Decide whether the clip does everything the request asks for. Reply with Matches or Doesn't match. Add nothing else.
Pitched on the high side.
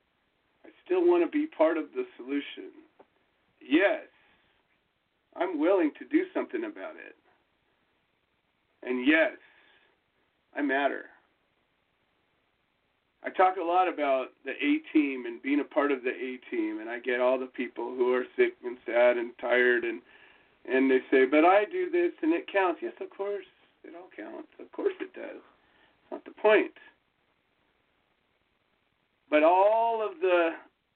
Matches